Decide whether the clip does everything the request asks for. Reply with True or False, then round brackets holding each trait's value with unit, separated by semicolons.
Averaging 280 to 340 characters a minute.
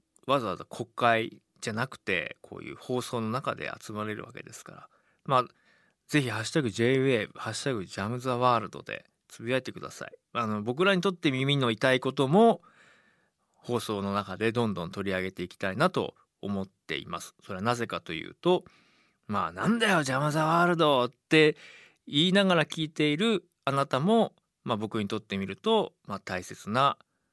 False (360 characters per minute)